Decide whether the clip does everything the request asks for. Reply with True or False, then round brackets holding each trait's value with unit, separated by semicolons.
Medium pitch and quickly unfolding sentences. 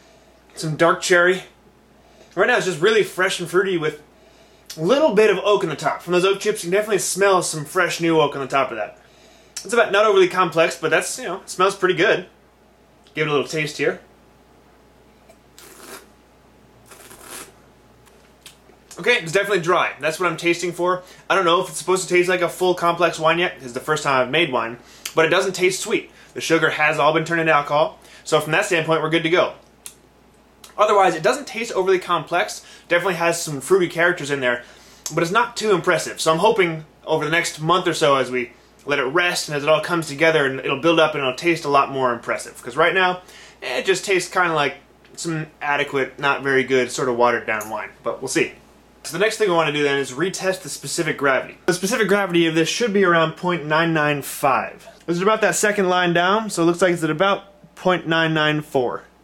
True (170 Hz; 220 wpm)